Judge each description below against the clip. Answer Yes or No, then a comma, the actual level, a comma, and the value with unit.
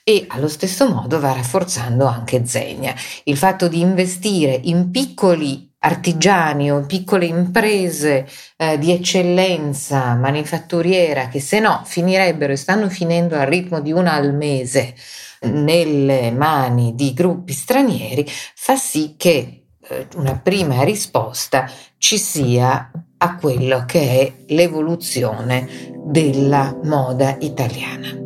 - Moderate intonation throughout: Yes, average, 4.8 semitones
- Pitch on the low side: No, medium, 155 Hz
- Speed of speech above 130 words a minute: No, average, 125 wpm